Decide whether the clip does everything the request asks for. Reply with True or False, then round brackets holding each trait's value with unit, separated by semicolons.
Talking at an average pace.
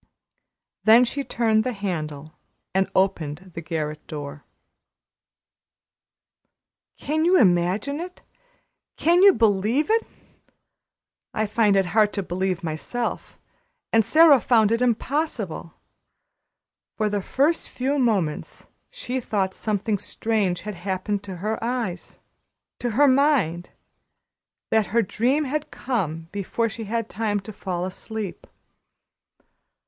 False (125 wpm)